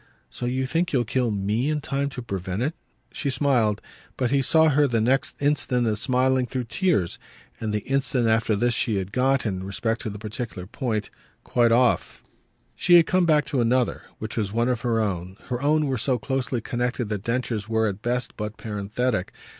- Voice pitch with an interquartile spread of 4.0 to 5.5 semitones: No, average, 3.6 semitones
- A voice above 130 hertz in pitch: No, low, 120 Hz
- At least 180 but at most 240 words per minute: Yes, average, 200 wpm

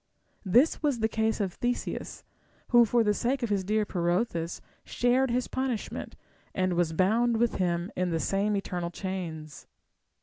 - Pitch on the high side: Yes, high, 210 Hz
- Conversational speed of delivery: Yes, average, 160 wpm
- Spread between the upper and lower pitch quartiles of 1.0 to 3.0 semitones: No, average, 5.1 semitones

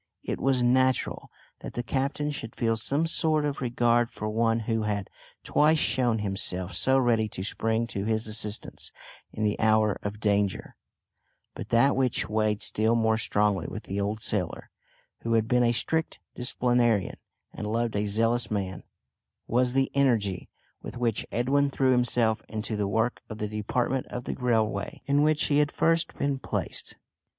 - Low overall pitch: Yes, low, 115 Hz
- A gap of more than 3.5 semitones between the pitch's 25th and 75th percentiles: No, average, 3.1 semitones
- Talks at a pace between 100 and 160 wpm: No, average, 170 wpm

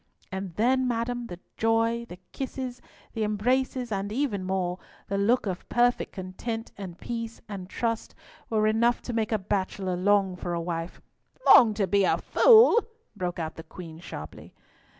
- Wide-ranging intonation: No, average, 4.2 semitones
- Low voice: No, high, 210 Hz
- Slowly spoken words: No, average, 160 wpm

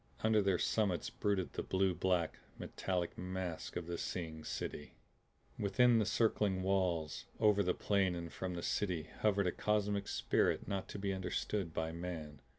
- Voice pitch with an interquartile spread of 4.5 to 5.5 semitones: No, average, 2.8 semitones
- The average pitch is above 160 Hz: No, very low, 95 Hz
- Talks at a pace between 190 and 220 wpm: No, average, 155 wpm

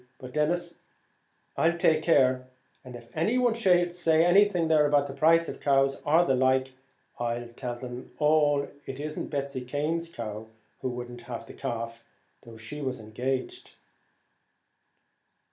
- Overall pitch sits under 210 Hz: Yes, medium, 140 Hz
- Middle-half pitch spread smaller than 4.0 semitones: No, average, 4.7 semitones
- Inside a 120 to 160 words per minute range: Yes, average, 145 wpm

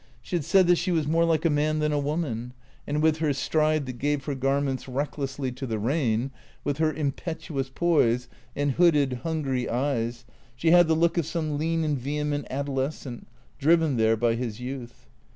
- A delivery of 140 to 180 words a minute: No, average, 190 wpm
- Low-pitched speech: No, medium, 145 Hz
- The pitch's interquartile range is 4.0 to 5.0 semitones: No, average, 3.6 semitones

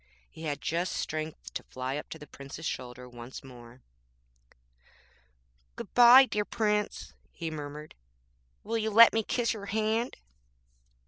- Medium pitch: Yes, medium, 145 Hz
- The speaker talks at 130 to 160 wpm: Yes, slow, 135 wpm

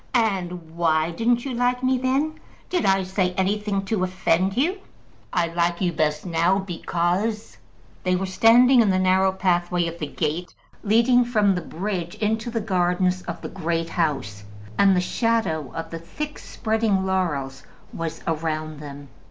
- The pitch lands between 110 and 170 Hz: No, medium, 185 Hz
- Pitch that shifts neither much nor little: Yes, average, 4.7 semitones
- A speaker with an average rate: Yes, average, 165 wpm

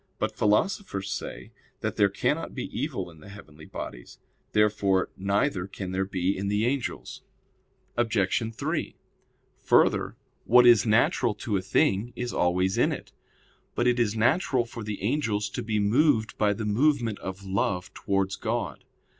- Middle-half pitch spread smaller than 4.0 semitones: Yes, average, 3.5 semitones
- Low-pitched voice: Yes, low, 105 Hz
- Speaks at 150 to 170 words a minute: Yes, average, 155 wpm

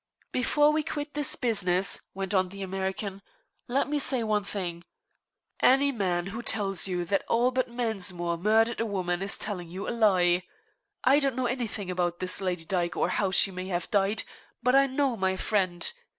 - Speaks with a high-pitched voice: Yes, high, 200 Hz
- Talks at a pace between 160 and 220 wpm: Yes, average, 185 wpm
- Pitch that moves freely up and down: No, average, 4.9 semitones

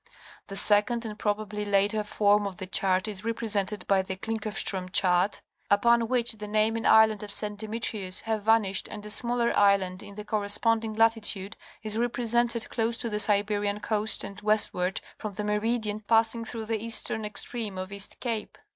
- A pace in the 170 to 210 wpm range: Yes, average, 175 wpm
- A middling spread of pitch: No, narrow, 1.8 semitones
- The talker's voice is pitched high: Yes, high, 210 Hz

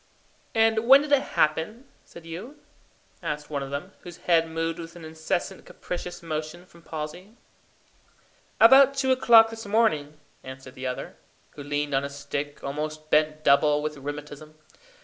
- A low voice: No, medium, 160 Hz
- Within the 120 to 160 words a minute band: Yes, average, 155 wpm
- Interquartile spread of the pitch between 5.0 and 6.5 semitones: Yes, wide, 5.4 semitones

